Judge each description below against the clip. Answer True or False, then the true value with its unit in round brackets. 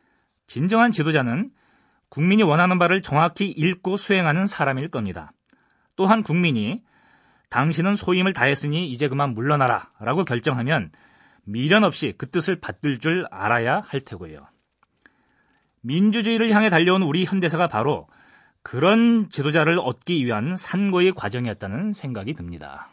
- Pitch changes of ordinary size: False (6.1 semitones)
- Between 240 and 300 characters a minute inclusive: False (310 characters per minute)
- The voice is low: False (170 Hz)